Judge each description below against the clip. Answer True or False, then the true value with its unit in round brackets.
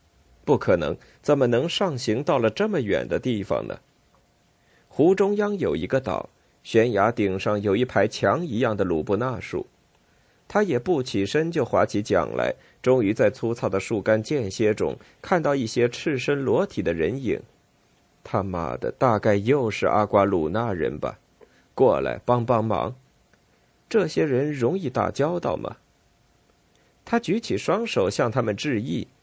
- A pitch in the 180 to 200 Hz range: False (120 Hz)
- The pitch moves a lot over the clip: True (6.2 semitones)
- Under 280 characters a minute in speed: True (225 characters per minute)